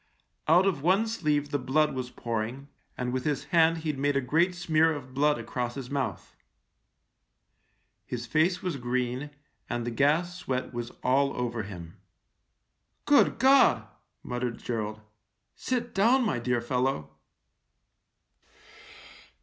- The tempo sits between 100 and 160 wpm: Yes, slow, 135 wpm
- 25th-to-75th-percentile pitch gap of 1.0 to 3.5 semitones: No, average, 5.1 semitones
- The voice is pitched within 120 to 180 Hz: Yes, medium, 140 Hz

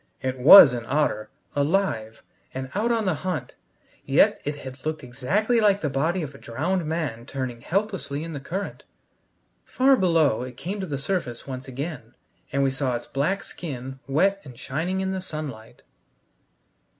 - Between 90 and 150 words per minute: No, average, 170 wpm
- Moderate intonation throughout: No, wide, 6.2 semitones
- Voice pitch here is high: No, medium, 145 Hz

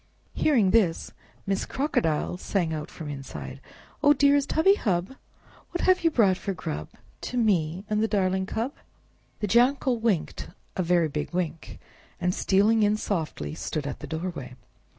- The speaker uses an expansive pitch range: Yes, wide, 6.1 semitones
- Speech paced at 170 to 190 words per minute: No, average, 155 wpm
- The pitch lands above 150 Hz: Yes, high, 190 Hz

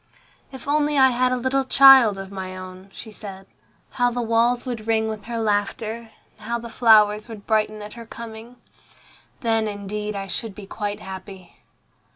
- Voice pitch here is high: Yes, high, 220 Hz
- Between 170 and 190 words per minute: Yes, average, 180 wpm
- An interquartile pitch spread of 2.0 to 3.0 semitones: Yes, average, 2.7 semitones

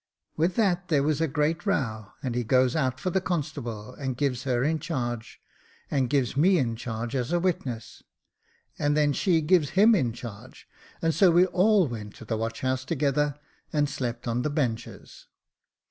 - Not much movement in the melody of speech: No, average, 5.2 semitones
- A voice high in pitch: No, medium, 140 Hz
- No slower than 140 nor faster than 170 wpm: No, average, 185 wpm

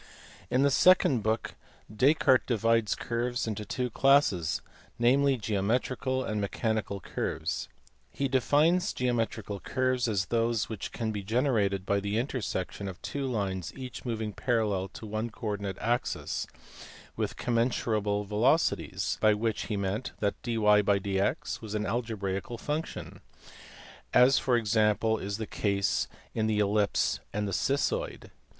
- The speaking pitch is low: Yes, low, 110 Hz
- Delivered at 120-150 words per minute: Yes, slow, 135 wpm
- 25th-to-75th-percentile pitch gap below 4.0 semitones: Yes, average, 3.5 semitones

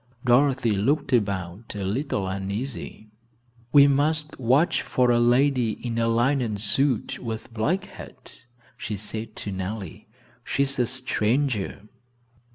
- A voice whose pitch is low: Yes, low, 120 Hz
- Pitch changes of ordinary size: Yes, average, 4.4 semitones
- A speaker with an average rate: No, slow, 125 wpm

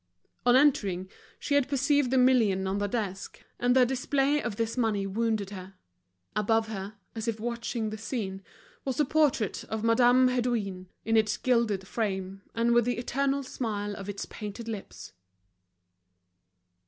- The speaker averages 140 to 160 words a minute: Yes, average, 155 wpm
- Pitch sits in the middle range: No, high, 225 Hz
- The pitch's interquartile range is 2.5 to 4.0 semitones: Yes, average, 3.7 semitones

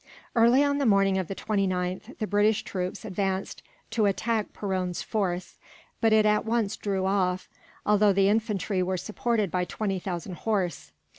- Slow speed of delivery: No, average, 160 wpm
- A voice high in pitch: Yes, high, 200 Hz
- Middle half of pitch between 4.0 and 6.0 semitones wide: No, narrow, 2.6 semitones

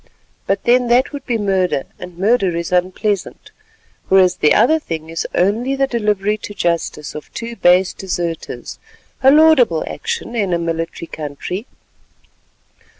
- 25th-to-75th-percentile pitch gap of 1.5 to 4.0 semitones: No, wide, 5.6 semitones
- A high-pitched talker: Yes, high, 195 Hz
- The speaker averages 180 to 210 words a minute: No, average, 145 wpm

